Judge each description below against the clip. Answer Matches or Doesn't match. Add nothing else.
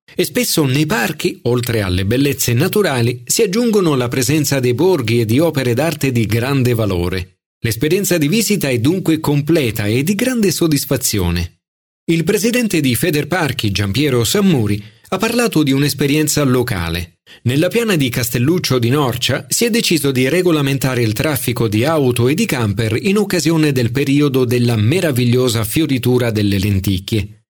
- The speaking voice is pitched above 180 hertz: Doesn't match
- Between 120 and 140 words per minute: Doesn't match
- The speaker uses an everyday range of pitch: Doesn't match